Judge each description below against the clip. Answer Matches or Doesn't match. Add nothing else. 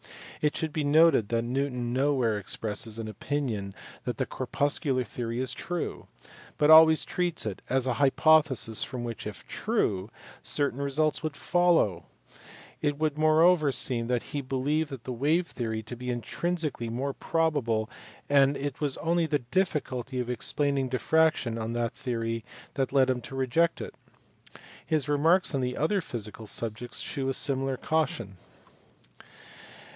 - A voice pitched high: Doesn't match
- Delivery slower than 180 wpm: Matches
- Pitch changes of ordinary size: Matches